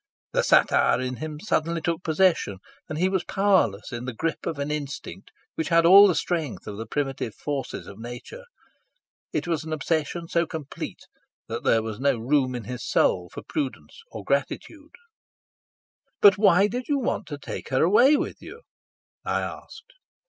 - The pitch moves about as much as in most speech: No, wide, 6.4 semitones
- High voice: No, medium, 155 Hz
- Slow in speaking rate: No, average, 175 wpm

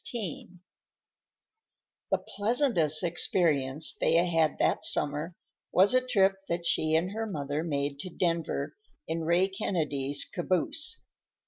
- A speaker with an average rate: No, slow, 120 wpm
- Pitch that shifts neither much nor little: Yes, average, 4.0 semitones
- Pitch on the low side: No, medium, 170 Hz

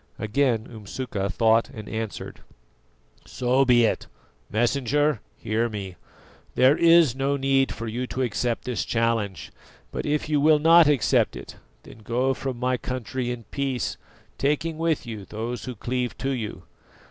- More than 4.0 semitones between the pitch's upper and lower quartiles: No, average, 3.3 semitones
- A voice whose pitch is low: Yes, low, 125 Hz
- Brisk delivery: No, average, 150 wpm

